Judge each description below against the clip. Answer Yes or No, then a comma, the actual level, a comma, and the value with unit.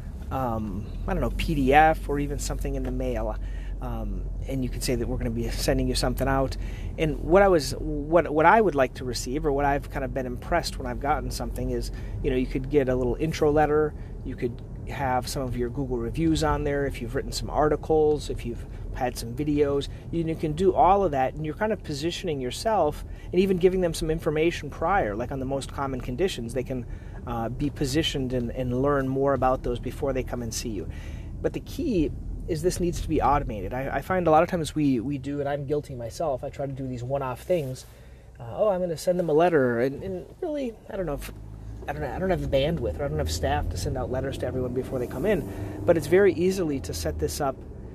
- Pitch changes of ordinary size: Yes, average, 4.2 semitones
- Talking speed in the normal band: No, fast, 245 wpm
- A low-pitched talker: Yes, low, 130 Hz